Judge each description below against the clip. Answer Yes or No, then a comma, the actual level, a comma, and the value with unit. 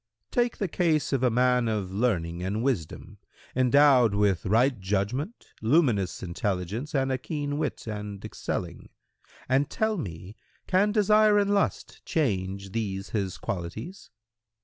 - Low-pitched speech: Yes, low, 120 Hz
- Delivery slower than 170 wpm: Yes, average, 140 wpm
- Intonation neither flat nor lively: No, wide, 7.3 semitones